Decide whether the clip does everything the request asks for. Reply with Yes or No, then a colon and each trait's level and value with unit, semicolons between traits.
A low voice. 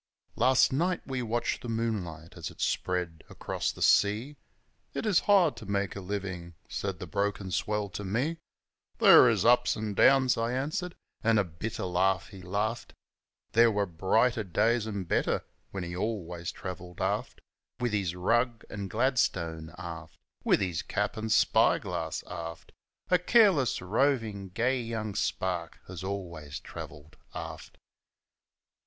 Yes: low, 100 Hz